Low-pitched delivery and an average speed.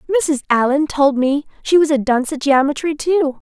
No: very high, 290 Hz; average, 190 wpm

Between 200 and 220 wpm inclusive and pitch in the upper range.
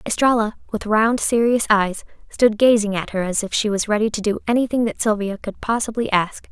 Yes: fast, 205 wpm; high, 215 Hz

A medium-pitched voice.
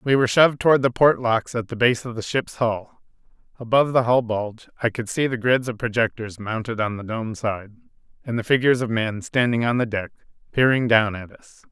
No: low, 115 Hz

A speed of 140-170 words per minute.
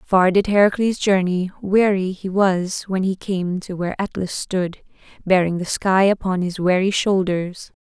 Yes: average, 160 wpm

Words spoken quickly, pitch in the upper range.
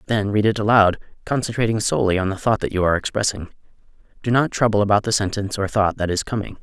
No: fast, 210 wpm; low, 105 Hz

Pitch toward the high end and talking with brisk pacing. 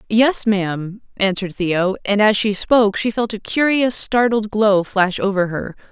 No: high, 205 Hz; average, 170 wpm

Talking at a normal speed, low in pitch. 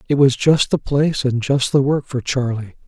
No: fast, 230 wpm; low, 130 Hz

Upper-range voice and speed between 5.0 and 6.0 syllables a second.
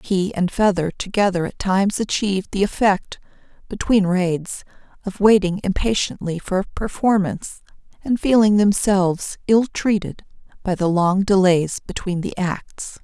No: high, 195 Hz; 4.5 syllables/s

